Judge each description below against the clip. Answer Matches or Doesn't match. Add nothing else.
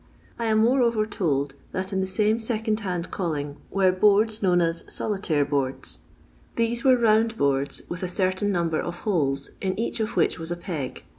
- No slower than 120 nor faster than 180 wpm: Doesn't match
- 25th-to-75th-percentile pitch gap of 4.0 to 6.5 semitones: Matches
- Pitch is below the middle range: Doesn't match